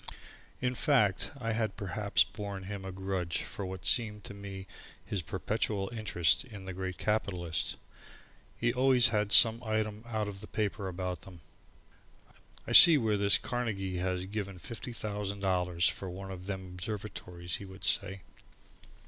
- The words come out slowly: No, average, 160 wpm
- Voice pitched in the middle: No, low, 100 Hz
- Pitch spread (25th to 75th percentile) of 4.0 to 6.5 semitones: No, narrow, 2.6 semitones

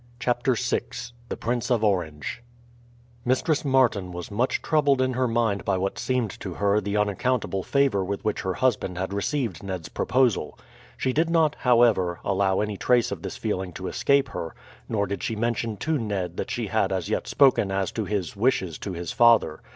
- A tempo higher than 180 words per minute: Yes, average, 190 wpm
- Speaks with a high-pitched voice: No, low, 105 Hz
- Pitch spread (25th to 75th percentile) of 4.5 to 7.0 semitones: Yes, average, 4.9 semitones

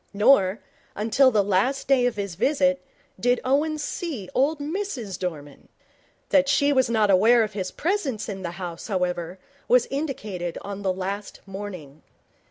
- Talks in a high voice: Yes, high, 215 Hz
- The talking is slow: No, average, 155 wpm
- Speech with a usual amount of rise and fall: No, wide, 6.4 semitones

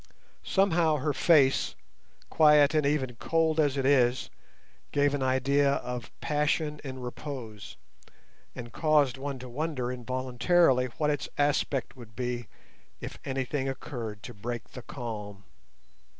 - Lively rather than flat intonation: No, average, 3.3 semitones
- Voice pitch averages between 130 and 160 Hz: Yes, low, 135 Hz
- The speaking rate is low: Yes, slow, 130 wpm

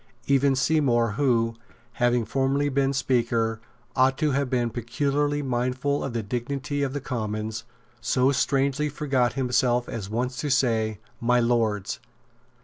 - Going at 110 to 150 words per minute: Yes, average, 140 wpm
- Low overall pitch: Yes, low, 125 Hz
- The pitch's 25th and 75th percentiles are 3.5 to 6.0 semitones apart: No, average, 2.9 semitones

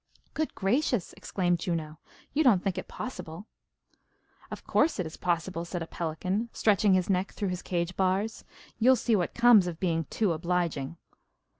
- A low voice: No, medium, 185 Hz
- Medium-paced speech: Yes, average, 165 wpm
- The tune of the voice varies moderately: Yes, average, 3.9 semitones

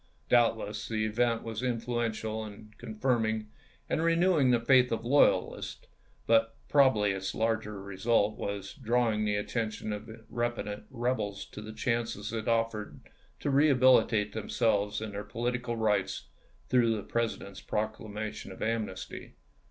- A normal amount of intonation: No, narrow, 2.2 semitones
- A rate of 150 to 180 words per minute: No, slow, 135 wpm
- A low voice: Yes, low, 110 Hz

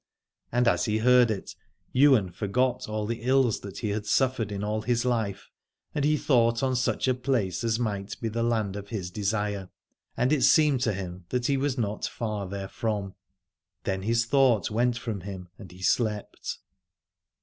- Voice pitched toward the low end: Yes, low, 110 Hz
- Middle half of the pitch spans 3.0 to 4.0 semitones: Yes, average, 3.7 semitones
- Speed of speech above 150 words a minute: Yes, average, 180 wpm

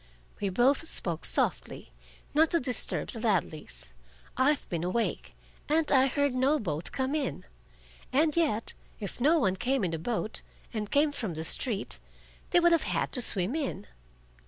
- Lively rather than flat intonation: Yes, wide, 7.4 semitones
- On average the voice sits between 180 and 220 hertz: No, high, 245 Hz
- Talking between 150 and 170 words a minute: Yes, average, 165 wpm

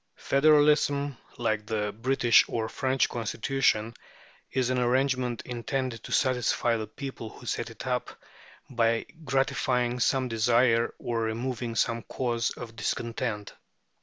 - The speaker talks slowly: Yes, slow, 125 wpm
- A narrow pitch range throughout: Yes, narrow, 2.3 semitones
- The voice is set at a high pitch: No, low, 120 Hz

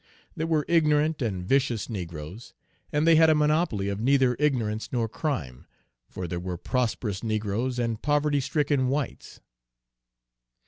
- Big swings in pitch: Yes, wide, 6.0 semitones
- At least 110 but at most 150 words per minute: Yes, average, 140 wpm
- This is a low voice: Yes, low, 125 Hz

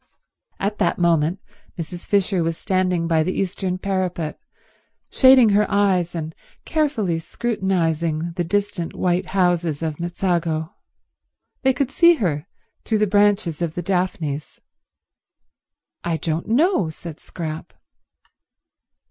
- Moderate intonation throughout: Yes, average, 3.4 semitones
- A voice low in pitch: No, medium, 180 Hz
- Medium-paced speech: No, slow, 120 wpm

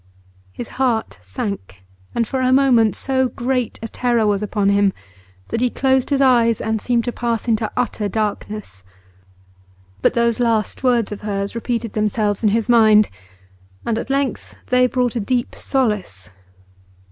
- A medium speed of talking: Yes, average, 160 wpm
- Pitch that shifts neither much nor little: Yes, average, 3.0 semitones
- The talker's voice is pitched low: No, high, 230 Hz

